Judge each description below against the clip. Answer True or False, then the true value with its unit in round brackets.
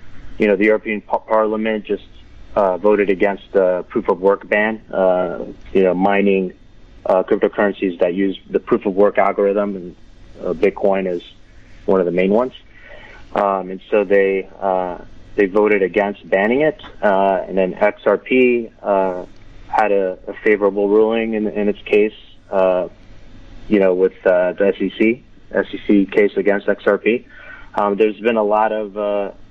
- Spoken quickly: False (160 wpm)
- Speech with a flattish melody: True (2.1 semitones)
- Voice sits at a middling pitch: False (100 Hz)